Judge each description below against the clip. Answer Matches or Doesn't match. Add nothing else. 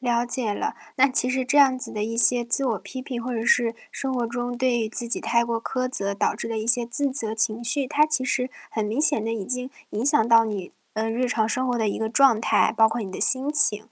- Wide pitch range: Doesn't match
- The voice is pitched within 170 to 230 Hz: Doesn't match